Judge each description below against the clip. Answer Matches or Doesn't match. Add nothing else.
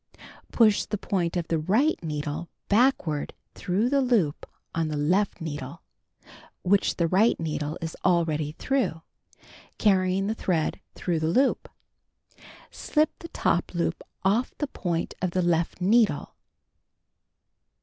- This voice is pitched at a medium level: Matches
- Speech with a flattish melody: Doesn't match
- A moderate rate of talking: Doesn't match